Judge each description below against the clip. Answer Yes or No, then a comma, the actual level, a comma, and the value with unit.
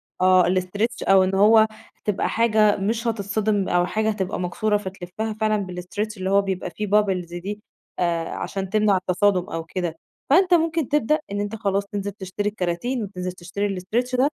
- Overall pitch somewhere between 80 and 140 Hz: No, high, 200 Hz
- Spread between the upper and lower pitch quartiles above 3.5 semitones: No, average, 2.8 semitones